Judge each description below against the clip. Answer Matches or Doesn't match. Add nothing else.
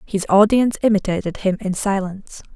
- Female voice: Matches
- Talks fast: Doesn't match